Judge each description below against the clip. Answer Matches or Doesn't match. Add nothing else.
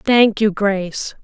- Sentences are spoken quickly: Doesn't match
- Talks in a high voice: Matches